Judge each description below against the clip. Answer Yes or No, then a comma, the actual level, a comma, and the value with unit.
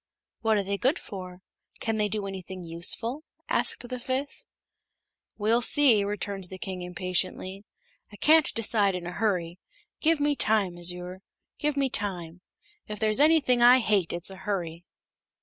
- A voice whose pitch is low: No, high, 205 Hz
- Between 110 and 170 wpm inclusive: Yes, average, 155 wpm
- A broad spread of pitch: No, average, 4.7 semitones